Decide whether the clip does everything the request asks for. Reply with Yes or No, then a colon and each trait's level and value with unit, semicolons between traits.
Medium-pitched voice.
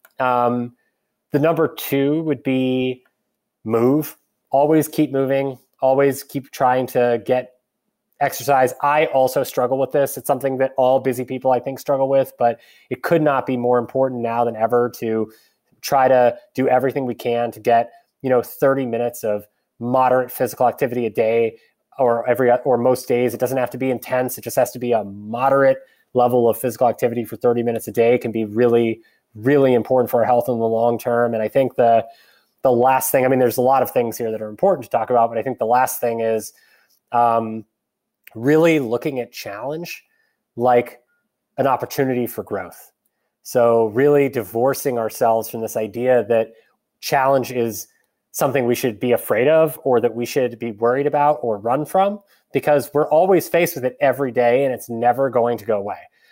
No: low, 125 Hz